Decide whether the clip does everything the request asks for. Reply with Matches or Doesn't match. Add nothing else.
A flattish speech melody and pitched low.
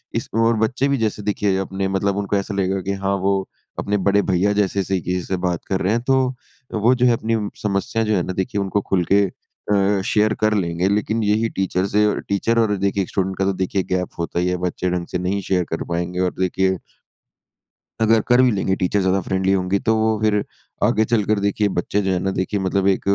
Matches